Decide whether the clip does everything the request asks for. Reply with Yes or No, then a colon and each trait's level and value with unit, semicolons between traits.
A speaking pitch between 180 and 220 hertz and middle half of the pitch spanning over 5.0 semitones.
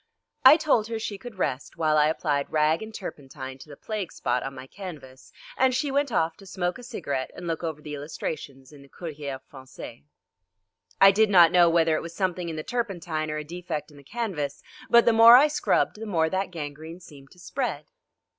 No: medium, 165 Hz; wide, 5.6 semitones